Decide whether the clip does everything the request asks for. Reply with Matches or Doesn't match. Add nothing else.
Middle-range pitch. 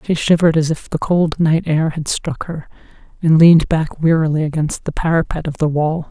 Matches